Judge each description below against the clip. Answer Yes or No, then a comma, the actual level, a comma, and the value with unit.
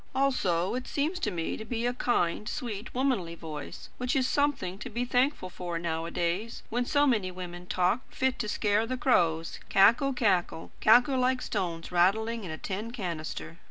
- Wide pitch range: Yes, wide, 6.2 semitones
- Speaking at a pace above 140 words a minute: Yes, average, 175 wpm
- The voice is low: No, high, 215 Hz